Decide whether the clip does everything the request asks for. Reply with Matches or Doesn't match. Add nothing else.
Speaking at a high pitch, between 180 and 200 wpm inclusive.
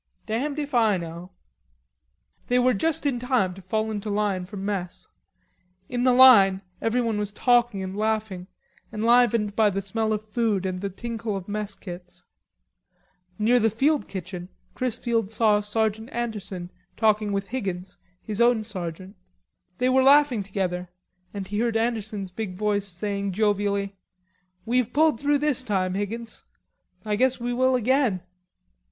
Doesn't match